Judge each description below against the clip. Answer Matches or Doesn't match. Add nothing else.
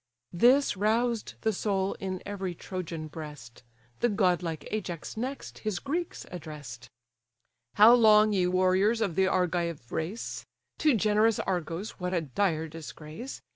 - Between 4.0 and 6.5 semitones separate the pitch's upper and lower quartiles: Matches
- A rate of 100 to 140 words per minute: Matches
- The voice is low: Doesn't match